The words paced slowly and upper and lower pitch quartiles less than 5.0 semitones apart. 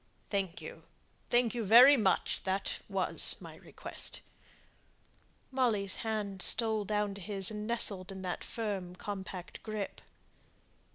Yes: slow, 125 wpm; narrow, 2.6 semitones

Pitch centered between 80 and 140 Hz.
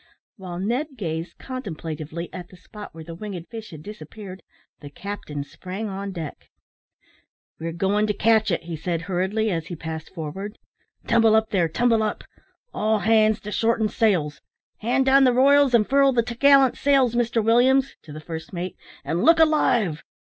No: high, 210 Hz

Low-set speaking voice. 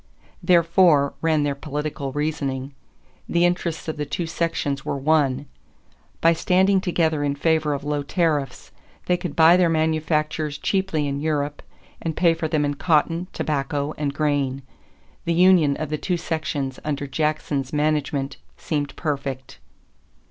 No: medium, 150 Hz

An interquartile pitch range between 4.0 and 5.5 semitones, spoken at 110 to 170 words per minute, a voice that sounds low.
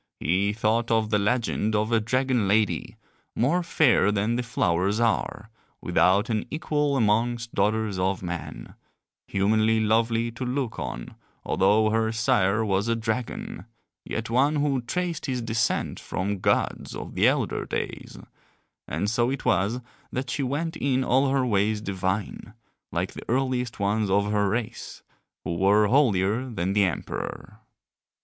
No: average, 3.4 semitones; average, 150 wpm; low, 110 Hz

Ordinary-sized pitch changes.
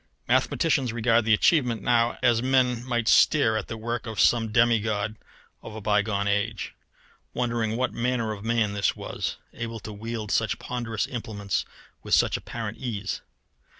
No: narrow, 1.9 semitones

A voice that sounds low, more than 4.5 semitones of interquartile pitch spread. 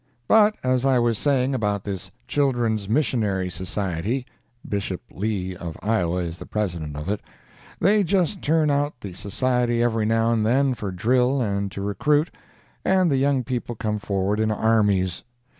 Yes: low, 110 Hz; average, 4.9 semitones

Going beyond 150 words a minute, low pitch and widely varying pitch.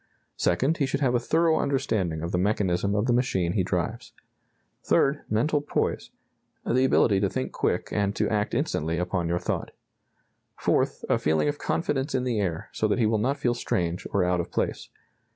Yes: average, 190 wpm; low, 105 Hz; wide, 6.8 semitones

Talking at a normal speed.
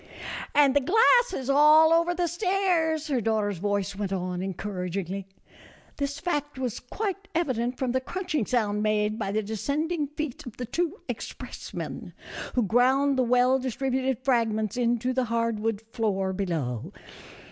Yes: average, 160 wpm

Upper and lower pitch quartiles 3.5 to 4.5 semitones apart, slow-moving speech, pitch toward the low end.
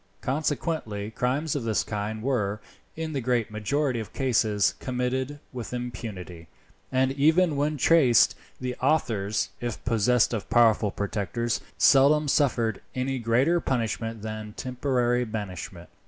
Yes: average, 3.8 semitones; slow, 125 wpm; low, 120 Hz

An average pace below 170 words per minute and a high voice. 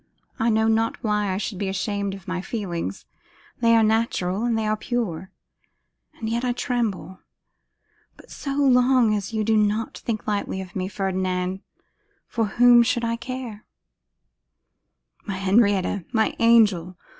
Yes: average, 150 wpm; high, 215 Hz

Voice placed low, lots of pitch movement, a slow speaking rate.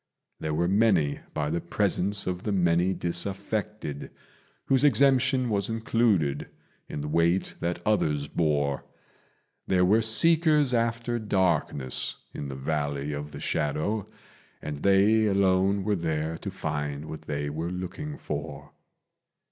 Yes: very low, 90 Hz; wide, 6.1 semitones; slow, 130 wpm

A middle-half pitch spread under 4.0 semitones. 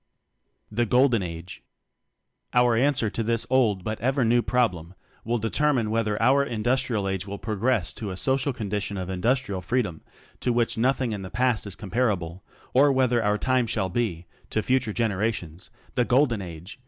No: average, 4.3 semitones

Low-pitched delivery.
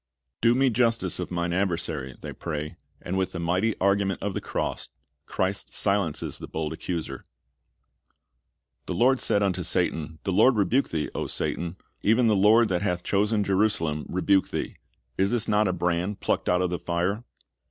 Yes: very low, 95 Hz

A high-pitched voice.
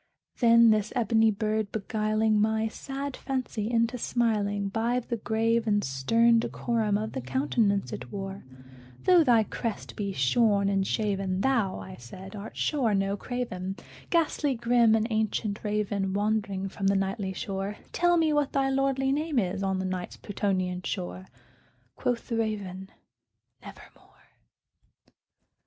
Yes: high, 215 Hz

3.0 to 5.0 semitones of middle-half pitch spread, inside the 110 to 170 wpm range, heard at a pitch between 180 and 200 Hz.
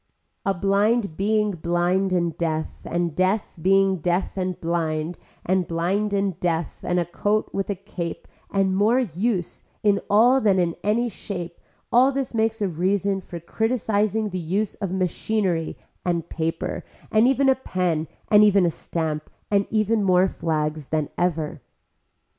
Yes: average, 3.5 semitones; average, 155 wpm; high, 190 Hz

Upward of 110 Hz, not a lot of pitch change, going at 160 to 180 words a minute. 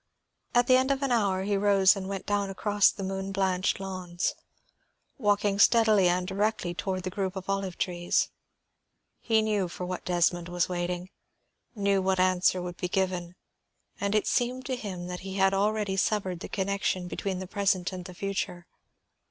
Yes: high, 190 Hz; narrow, 2.1 semitones; average, 175 wpm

